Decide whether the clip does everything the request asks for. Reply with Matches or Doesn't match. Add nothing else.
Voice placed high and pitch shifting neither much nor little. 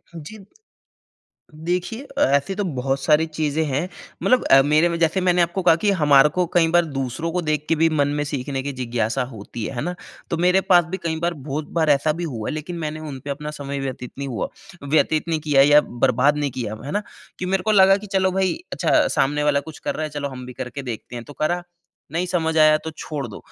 Doesn't match